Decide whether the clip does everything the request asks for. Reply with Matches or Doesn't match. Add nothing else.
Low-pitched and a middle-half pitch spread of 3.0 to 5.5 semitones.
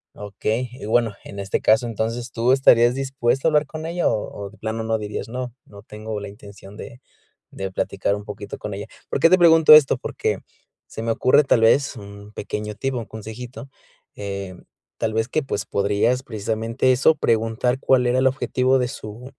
Matches